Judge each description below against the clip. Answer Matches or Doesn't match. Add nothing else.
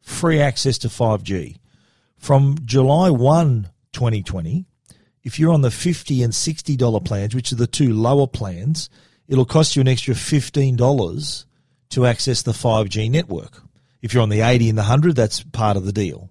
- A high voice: Doesn't match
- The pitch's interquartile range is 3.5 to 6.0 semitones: Matches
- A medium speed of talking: Matches